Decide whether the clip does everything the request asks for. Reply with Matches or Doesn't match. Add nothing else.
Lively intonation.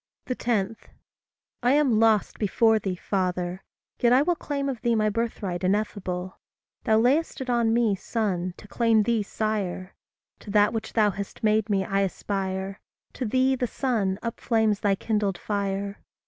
Doesn't match